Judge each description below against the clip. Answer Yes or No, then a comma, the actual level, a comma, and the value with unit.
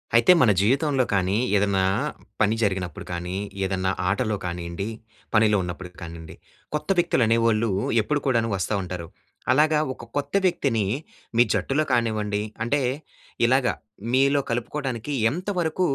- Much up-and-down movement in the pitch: Yes, wide, 6.3 semitones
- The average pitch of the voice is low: Yes, low, 115 Hz